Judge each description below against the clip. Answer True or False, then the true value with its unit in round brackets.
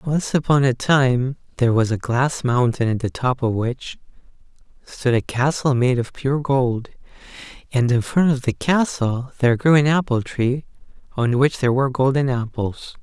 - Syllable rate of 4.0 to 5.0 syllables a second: True (4.7 syllables/s)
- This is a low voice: True (130 Hz)